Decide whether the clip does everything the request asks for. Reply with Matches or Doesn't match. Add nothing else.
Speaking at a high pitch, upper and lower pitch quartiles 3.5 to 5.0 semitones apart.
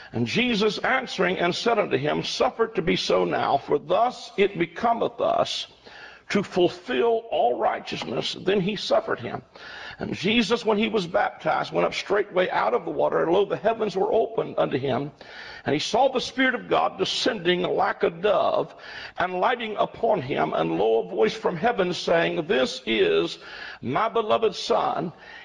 Matches